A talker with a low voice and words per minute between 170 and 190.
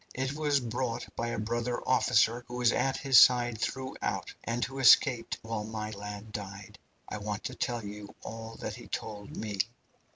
Yes: low, 115 Hz; average, 175 wpm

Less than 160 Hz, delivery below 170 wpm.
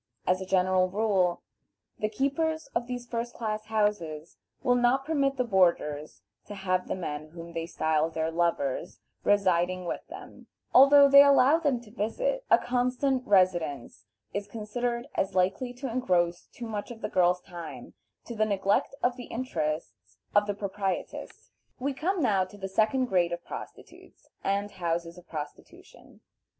No: high, 205 Hz; average, 160 wpm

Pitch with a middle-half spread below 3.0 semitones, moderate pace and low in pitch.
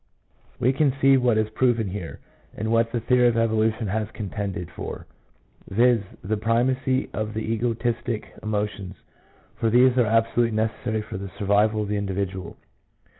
Yes: narrow, 2.4 semitones; average, 160 wpm; low, 110 Hz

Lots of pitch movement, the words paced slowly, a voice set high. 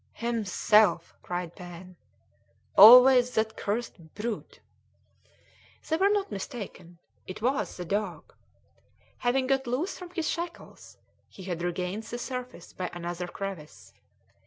Yes: wide, 5.9 semitones; slow, 120 wpm; high, 215 Hz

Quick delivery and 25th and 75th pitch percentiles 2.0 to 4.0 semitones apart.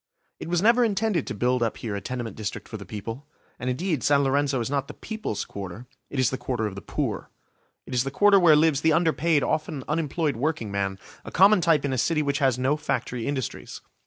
No: fast, 220 wpm; average, 5.2 semitones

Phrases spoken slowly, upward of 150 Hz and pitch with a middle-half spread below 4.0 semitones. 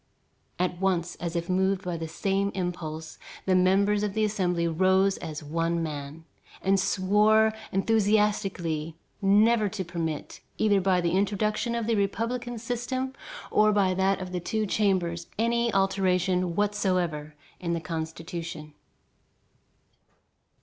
Yes: slow, 130 wpm; high, 190 Hz; average, 3.5 semitones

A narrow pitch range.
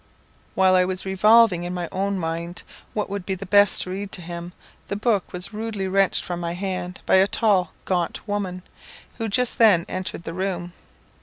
Yes: narrow, 2.2 semitones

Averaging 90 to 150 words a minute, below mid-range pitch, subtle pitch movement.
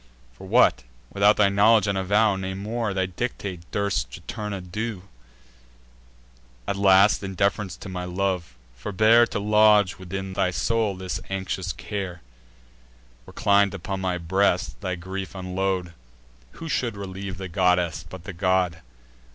Yes: average, 140 wpm; very low, 95 Hz; narrow, 2.0 semitones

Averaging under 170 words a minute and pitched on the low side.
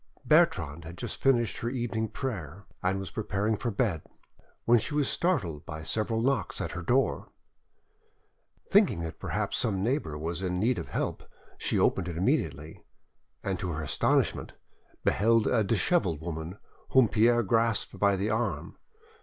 Yes: average, 155 wpm; low, 105 Hz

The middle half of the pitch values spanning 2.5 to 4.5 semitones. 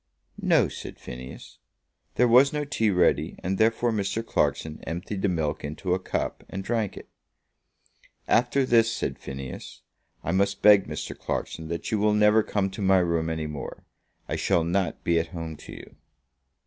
No: average, 5.0 semitones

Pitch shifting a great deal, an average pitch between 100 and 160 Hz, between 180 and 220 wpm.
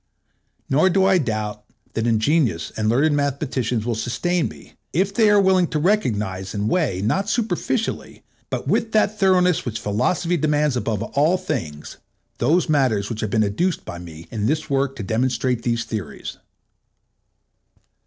No: wide, 8.5 semitones; low, 135 Hz; average, 155 wpm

